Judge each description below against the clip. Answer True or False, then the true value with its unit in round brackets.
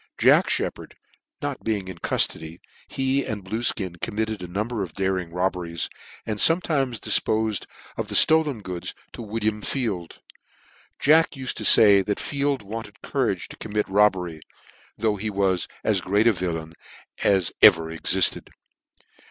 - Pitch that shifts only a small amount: False (3.8 semitones)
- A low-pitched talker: True (105 Hz)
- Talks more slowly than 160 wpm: True (145 wpm)